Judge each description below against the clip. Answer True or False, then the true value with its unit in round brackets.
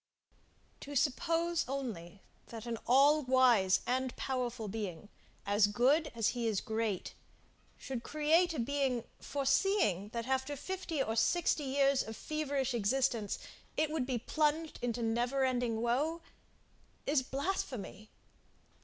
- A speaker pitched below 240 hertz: False (255 Hz)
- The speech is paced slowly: True (125 wpm)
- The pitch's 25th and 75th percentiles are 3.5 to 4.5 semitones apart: True (4.1 semitones)